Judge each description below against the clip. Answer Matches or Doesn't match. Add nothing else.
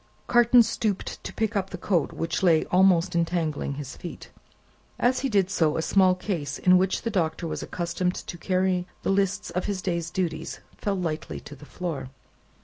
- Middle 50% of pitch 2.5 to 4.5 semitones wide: Matches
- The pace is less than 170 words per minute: Doesn't match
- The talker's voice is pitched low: Doesn't match